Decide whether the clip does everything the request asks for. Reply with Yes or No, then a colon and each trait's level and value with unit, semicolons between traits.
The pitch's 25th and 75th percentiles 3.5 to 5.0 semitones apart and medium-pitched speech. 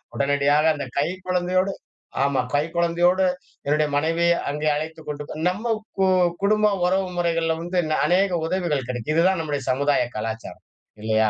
Yes: average, 4.0 semitones; medium, 160 Hz